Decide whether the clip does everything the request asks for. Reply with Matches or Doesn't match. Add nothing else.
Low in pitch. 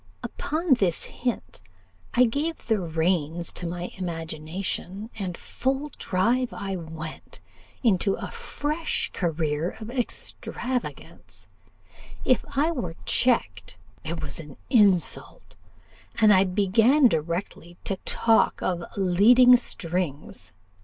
Doesn't match